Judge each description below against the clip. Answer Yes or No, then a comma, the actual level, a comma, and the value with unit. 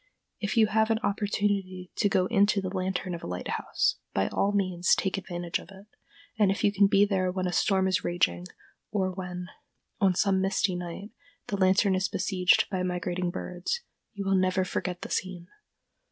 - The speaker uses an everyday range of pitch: No, narrow, 1.7 semitones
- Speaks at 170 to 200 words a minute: Yes, average, 185 wpm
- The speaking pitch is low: No, high, 190 Hz